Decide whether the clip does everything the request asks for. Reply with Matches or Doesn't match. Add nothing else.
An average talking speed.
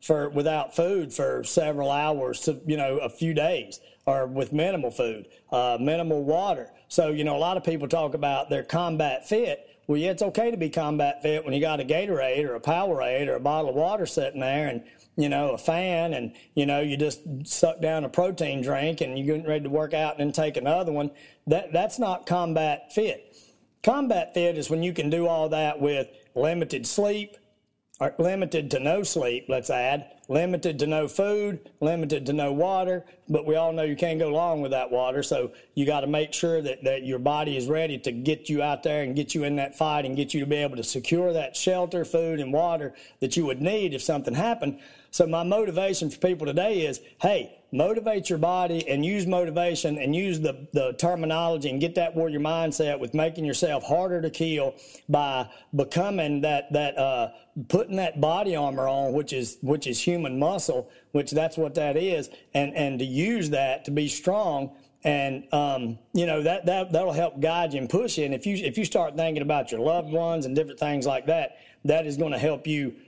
Doesn't match